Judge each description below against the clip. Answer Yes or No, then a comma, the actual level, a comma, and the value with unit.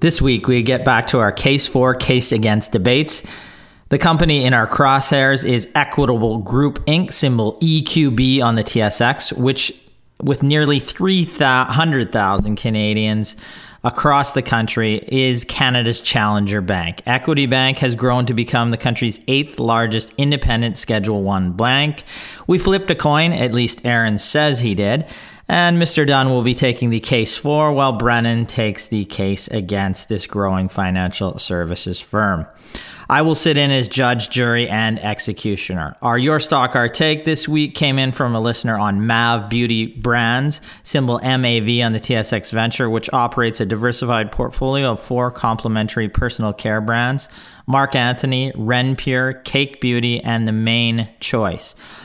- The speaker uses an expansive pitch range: No, average, 3.5 semitones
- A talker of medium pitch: No, low, 120 Hz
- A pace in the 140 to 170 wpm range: Yes, average, 155 wpm